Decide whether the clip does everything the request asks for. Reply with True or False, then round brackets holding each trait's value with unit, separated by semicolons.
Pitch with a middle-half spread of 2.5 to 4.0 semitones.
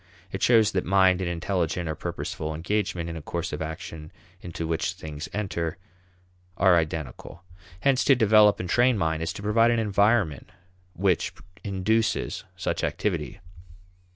False (4.4 semitones)